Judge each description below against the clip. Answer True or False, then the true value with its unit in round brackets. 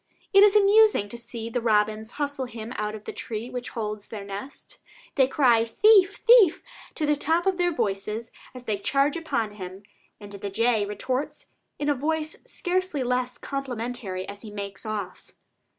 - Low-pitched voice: False (245 Hz)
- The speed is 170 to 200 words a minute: True (175 wpm)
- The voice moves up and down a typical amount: False (5.9 semitones)